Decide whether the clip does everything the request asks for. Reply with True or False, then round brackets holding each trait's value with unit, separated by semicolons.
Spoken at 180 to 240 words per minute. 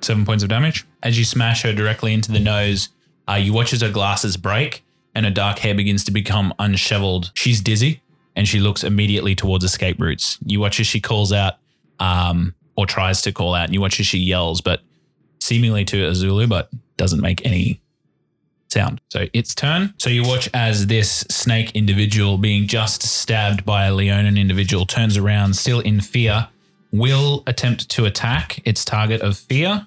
True (185 wpm)